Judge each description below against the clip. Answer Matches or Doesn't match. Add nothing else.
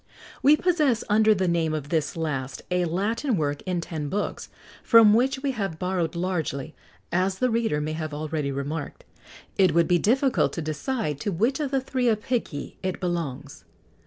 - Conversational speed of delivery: Matches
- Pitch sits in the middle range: Matches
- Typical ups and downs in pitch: Doesn't match